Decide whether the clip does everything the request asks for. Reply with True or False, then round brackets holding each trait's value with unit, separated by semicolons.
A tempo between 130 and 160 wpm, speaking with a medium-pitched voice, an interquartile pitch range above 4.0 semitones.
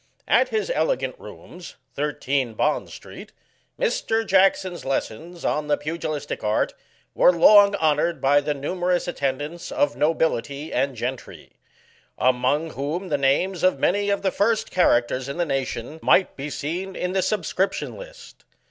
True (145 wpm; 160 Hz; 5.1 semitones)